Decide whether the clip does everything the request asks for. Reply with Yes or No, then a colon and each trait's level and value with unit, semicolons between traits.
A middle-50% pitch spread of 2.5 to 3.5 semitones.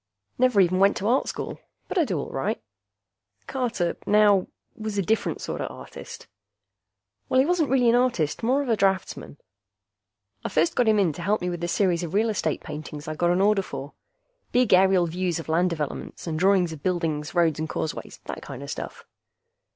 No: average, 5.0 semitones